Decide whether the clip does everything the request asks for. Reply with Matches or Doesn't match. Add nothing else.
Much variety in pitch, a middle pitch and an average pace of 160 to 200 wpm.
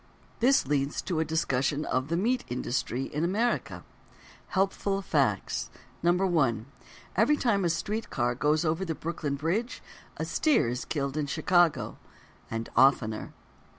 Doesn't match